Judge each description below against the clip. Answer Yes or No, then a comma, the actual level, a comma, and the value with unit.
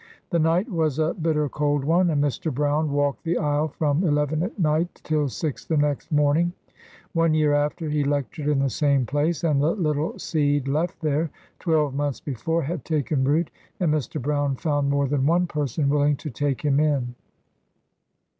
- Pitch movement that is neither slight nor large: No, narrow, 2.0 semitones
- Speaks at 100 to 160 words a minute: No, average, 185 wpm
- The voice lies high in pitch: No, medium, 150 Hz